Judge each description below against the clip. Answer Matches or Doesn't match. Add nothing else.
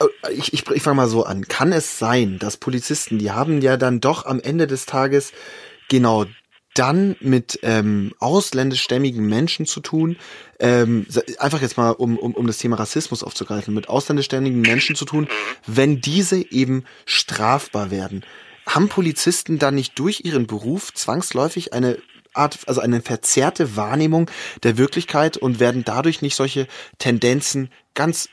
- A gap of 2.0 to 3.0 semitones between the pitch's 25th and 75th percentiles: Doesn't match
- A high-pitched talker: Doesn't match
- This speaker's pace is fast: Doesn't match